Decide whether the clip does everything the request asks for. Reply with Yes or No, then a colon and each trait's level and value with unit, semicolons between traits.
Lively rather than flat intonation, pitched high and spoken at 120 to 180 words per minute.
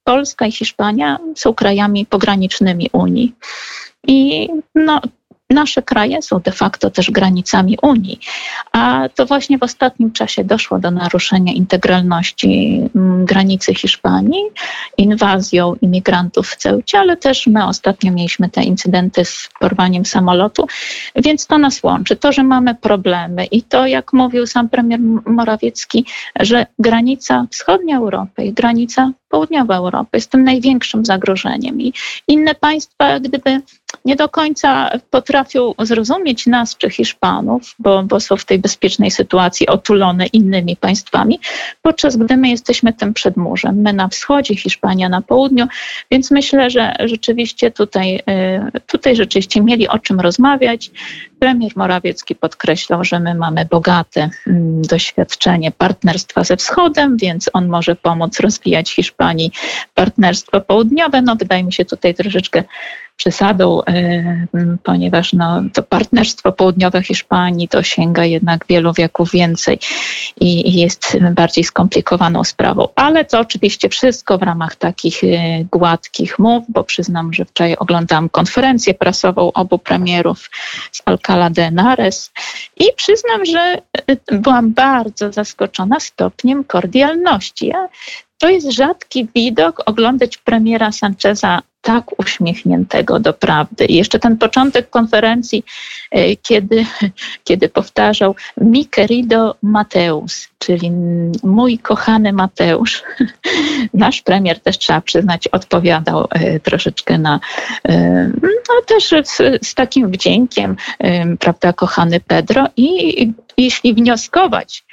Yes: wide, 5.8 semitones; high, 215 Hz; average, 125 wpm